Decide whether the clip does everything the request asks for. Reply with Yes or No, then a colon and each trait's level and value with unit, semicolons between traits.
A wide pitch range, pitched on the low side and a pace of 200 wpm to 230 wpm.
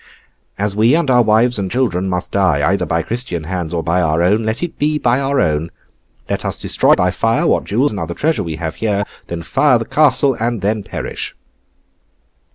Yes: wide, 6.3 semitones; low, 105 Hz; fast, 205 wpm